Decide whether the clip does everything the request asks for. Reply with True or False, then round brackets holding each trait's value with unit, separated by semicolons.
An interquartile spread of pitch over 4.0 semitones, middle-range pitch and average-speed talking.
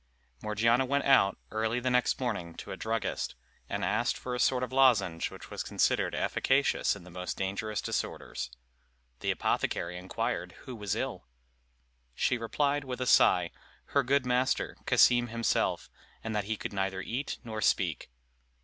False (4.6 semitones; 115 Hz; 160 wpm)